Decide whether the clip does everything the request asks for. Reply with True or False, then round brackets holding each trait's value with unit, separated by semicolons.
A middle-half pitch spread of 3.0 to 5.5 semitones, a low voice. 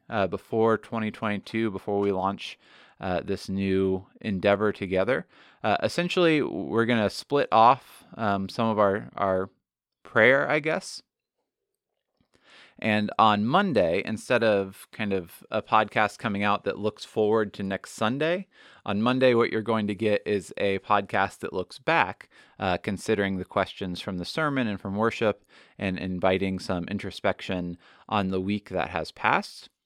False (2.4 semitones; 100 Hz)